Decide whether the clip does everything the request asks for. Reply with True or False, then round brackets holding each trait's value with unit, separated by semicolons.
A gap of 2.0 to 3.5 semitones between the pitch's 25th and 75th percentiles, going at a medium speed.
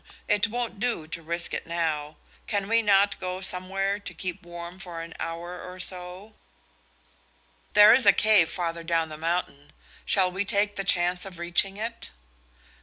True (3.0 semitones; 170 wpm)